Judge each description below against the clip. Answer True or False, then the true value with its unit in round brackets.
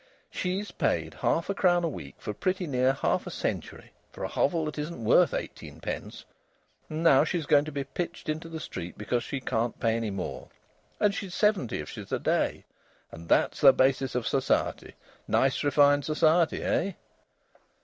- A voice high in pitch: False (145 Hz)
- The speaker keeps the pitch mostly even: False (4.9 semitones)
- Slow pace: False (180 wpm)